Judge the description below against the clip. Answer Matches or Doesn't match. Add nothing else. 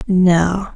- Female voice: Matches